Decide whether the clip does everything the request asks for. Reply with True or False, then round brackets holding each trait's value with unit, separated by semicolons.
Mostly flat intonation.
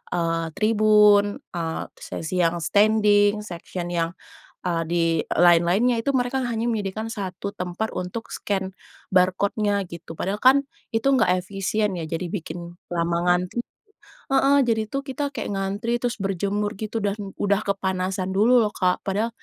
False (3.5 semitones)